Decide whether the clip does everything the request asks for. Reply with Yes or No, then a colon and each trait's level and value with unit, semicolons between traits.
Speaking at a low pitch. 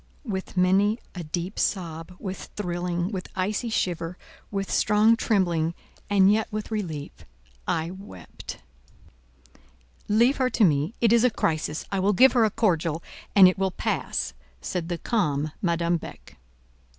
No: medium, 185 Hz